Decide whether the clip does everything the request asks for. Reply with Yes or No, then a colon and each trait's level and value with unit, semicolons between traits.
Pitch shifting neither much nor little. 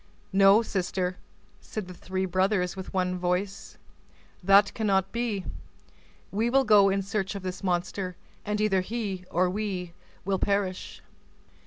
No: narrow, 2.0 semitones